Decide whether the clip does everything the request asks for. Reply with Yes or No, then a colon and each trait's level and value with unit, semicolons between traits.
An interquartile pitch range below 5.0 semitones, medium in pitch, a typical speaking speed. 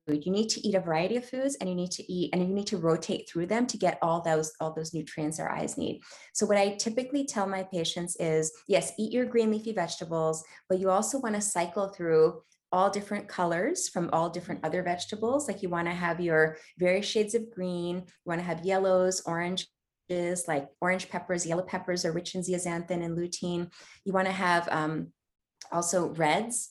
No: average, 2.8 semitones; medium, 180 Hz; fast, 210 wpm